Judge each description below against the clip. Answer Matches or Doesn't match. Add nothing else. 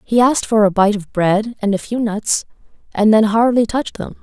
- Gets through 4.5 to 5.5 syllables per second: Matches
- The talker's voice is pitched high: Matches